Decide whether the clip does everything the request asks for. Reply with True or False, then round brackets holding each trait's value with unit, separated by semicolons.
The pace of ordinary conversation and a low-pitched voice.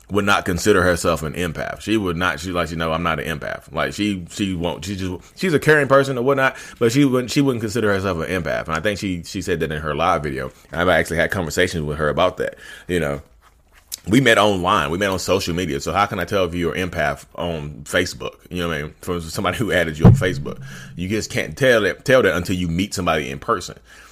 False (255 wpm; 90 Hz)